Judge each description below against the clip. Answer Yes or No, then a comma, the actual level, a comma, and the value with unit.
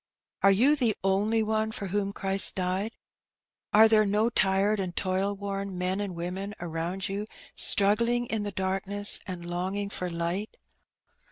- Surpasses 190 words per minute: No, average, 160 wpm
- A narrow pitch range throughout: Yes, narrow, 2.1 semitones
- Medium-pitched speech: No, high, 195 Hz